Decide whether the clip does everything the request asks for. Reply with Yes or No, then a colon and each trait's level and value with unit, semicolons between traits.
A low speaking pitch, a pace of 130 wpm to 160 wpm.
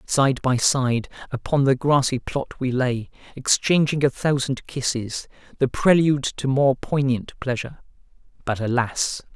Yes: low, 130 Hz; slow, 135 wpm